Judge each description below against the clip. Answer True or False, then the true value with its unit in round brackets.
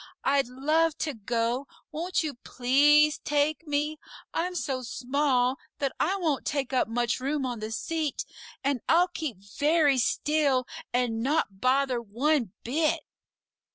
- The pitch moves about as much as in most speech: True (3.6 semitones)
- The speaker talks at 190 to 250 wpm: False (140 wpm)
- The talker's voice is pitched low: False (280 Hz)